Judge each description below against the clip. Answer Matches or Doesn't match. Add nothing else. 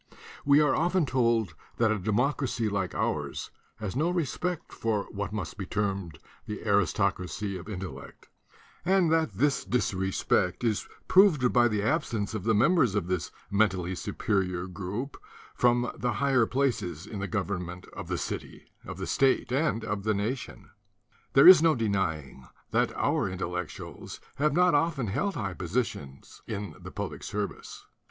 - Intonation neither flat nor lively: Doesn't match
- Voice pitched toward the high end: Doesn't match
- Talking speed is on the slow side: Doesn't match